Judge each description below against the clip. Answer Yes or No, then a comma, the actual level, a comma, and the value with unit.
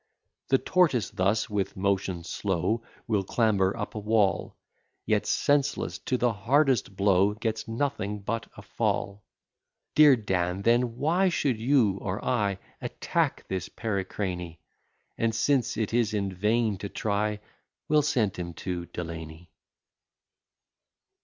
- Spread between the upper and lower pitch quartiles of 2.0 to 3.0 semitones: No, average, 3.8 semitones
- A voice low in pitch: Yes, low, 105 Hz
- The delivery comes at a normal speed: No, slow, 130 wpm